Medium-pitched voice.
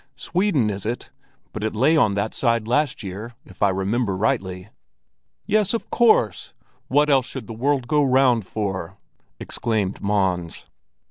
No: low, 110 Hz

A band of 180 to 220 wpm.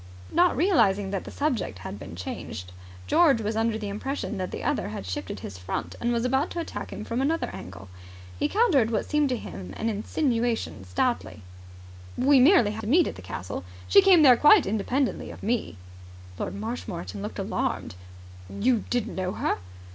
Yes: average, 185 wpm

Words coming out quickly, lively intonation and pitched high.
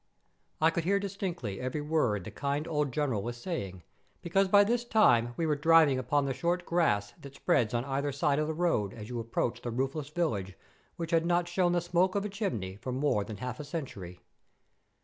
No: fast, 210 wpm; wide, 6.2 semitones; medium, 145 Hz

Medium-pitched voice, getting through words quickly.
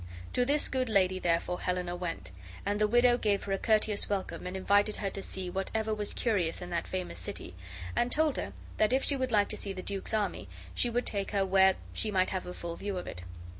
No: high, 200 Hz; fast, 235 wpm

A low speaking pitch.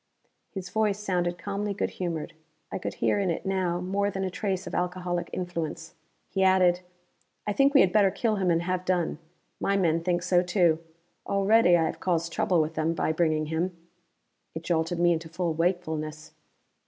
No: medium, 180 Hz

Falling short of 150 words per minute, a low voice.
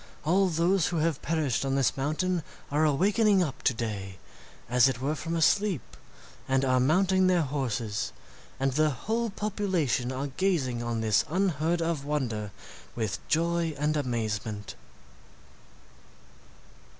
No: average, 140 wpm; medium, 150 Hz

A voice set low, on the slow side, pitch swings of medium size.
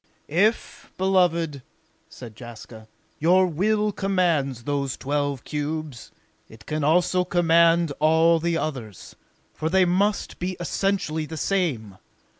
No: medium, 160 Hz; slow, 115 wpm; average, 4.1 semitones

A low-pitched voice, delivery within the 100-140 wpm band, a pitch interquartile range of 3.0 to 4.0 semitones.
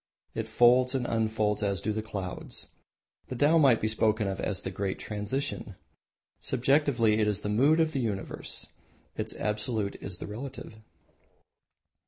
No: low, 110 Hz; average, 155 wpm; average, 3.5 semitones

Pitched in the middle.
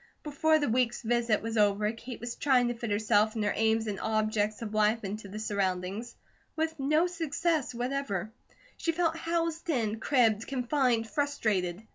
No: high, 230 Hz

